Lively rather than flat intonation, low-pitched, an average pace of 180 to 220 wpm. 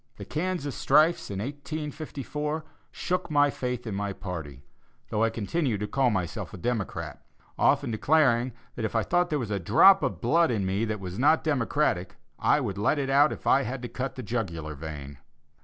Yes: wide, 6.7 semitones; low, 120 Hz; average, 190 wpm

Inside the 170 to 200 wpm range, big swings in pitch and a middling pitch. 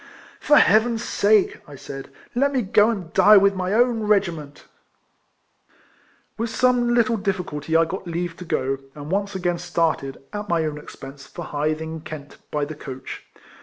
Yes: average, 185 wpm; wide, 5.7 semitones; medium, 180 Hz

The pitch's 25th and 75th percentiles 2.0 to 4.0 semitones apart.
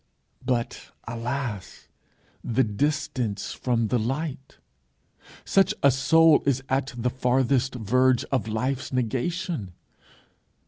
Yes: average, 2.8 semitones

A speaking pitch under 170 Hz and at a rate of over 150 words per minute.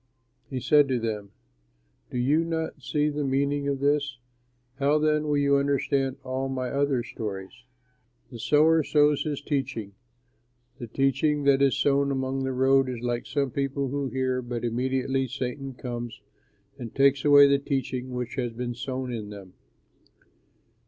Yes: low, 135 Hz; average, 160 wpm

